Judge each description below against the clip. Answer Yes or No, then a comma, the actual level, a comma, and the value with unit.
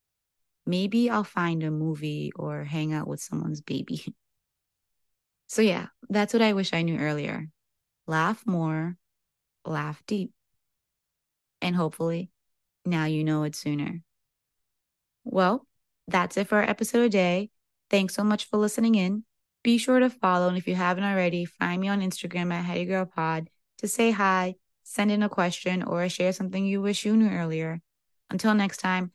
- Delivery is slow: No, average, 160 wpm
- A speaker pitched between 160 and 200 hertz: Yes, medium, 185 Hz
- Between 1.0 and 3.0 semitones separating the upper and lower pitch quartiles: No, average, 4.0 semitones